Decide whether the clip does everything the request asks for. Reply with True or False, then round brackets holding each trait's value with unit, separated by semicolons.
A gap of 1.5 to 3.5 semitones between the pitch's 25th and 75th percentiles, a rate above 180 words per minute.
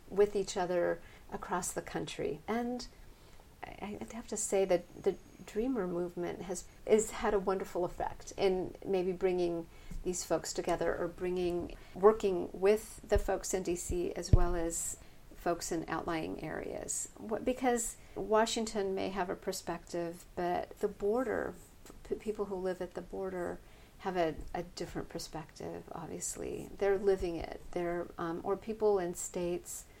False (2.8 semitones; 145 wpm)